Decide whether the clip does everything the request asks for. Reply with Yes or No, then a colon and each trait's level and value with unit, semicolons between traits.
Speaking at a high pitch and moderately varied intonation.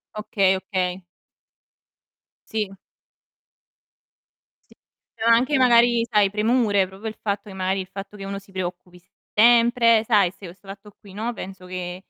Yes: high, 200 Hz; average, 3.0 semitones